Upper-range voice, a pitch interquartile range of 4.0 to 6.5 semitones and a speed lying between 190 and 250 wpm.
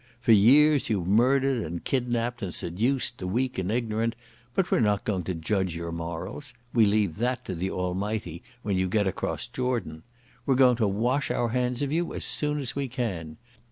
No: low, 110 Hz; average, 5.2 semitones; average, 195 wpm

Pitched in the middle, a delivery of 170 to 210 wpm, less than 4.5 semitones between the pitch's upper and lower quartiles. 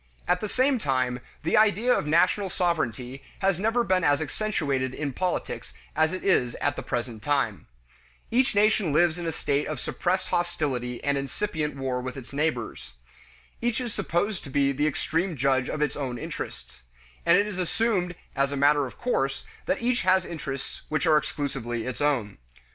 No: medium, 150 Hz; average, 175 wpm; wide, 5.6 semitones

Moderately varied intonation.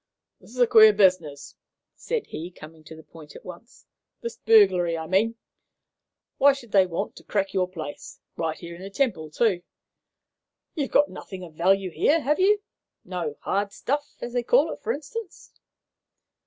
No: wide, 8.2 semitones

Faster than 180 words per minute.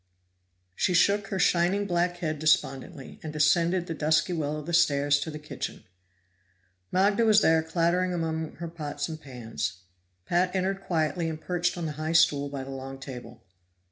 No: average, 170 wpm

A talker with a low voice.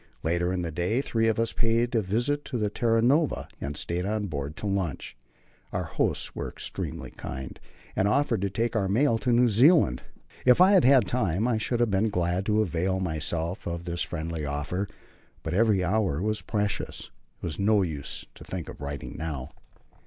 Yes: low, 100 Hz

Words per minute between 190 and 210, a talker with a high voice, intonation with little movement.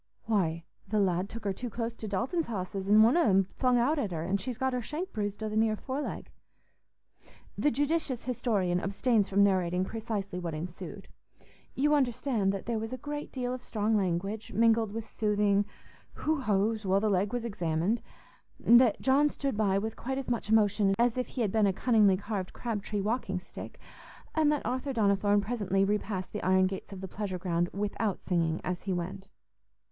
No: average, 195 wpm; high, 210 Hz; average, 3.9 semitones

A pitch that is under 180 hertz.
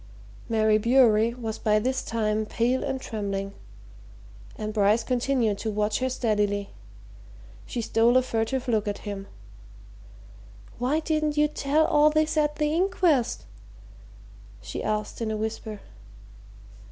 No: high, 230 Hz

